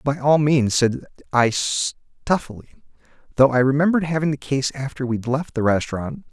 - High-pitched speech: No, low, 135 Hz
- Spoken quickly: No, average, 160 wpm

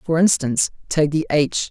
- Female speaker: No, male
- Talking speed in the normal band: Yes, average, 175 wpm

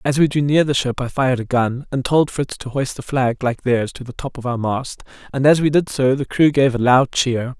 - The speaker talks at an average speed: No, fast, 285 wpm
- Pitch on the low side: Yes, low, 130 Hz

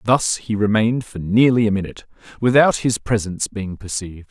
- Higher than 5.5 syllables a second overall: Yes, 5.8 syllables/s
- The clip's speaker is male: Yes, male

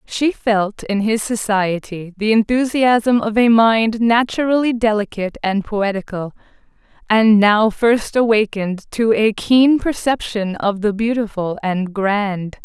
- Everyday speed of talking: No, slow, 130 wpm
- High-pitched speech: Yes, high, 215 Hz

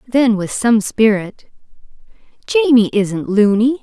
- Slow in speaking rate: Yes, slow, 110 wpm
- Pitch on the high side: Yes, high, 225 Hz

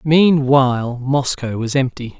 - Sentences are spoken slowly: Yes, slow, 110 wpm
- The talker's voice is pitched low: Yes, low, 130 Hz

